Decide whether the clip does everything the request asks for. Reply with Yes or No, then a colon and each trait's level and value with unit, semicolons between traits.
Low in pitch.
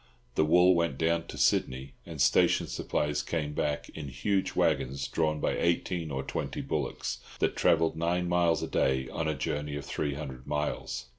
Yes: very low, 75 Hz